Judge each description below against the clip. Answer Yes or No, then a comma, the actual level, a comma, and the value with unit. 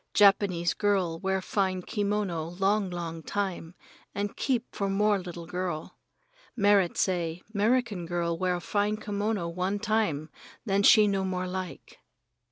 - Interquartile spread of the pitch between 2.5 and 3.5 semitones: Yes, average, 2.8 semitones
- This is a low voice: No, high, 190 Hz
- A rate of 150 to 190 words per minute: No, average, 140 wpm